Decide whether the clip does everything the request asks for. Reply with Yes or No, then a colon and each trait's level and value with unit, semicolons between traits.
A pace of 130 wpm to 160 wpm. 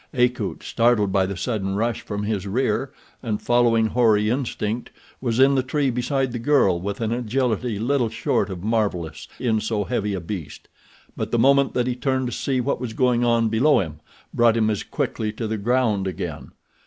No: average, 190 wpm